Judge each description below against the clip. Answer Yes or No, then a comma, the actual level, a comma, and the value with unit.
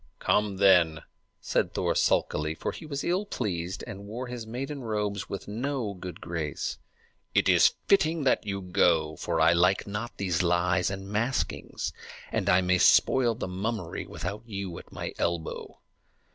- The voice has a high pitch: No, low, 100 Hz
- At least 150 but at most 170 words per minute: Yes, average, 160 wpm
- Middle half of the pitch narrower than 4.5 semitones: No, average, 4.8 semitones